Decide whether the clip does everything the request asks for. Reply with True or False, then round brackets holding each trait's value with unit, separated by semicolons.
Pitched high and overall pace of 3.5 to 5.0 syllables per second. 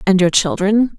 True (200 Hz; 4.8 syllables/s)